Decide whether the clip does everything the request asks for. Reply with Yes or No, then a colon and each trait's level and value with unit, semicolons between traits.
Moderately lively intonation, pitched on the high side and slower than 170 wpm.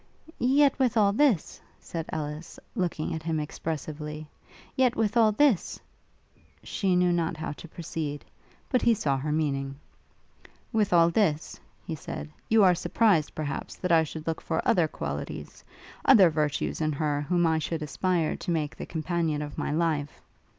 No: average, 4.3 semitones; medium, 165 Hz; average, 160 wpm